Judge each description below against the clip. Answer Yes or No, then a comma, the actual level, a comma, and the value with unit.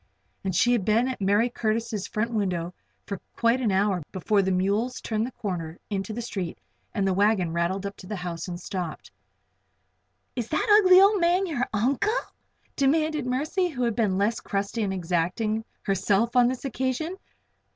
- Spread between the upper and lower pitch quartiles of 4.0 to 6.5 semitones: Yes, average, 4.8 semitones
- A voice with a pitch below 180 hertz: No, high, 215 Hz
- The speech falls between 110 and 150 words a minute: No, average, 180 wpm